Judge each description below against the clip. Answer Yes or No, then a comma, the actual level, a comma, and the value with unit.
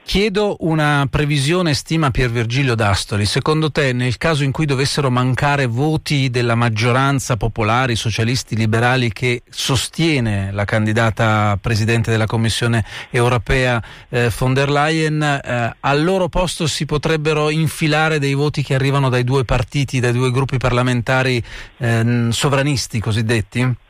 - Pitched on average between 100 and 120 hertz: No, low, 130 Hz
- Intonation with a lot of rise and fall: No, average, 3.9 semitones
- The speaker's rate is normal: Yes, average, 135 wpm